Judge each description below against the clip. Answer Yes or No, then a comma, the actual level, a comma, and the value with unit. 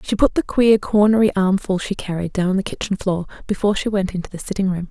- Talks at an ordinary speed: No, fast, 245 wpm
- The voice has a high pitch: Yes, high, 195 Hz